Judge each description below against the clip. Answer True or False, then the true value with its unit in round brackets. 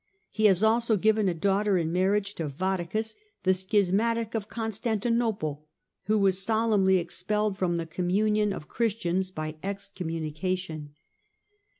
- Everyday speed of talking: False (130 wpm)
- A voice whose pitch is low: False (195 Hz)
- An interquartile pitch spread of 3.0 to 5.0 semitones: True (3.4 semitones)